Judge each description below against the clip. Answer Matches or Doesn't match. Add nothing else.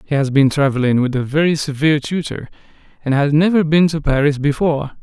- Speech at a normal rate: Matches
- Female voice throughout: Doesn't match